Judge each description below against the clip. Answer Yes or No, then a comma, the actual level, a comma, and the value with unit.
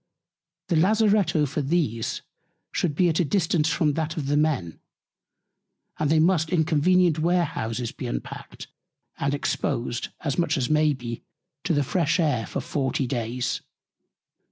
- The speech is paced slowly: No, average, 150 wpm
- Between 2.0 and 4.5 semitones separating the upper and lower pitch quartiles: Yes, average, 4.0 semitones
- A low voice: No, medium, 155 Hz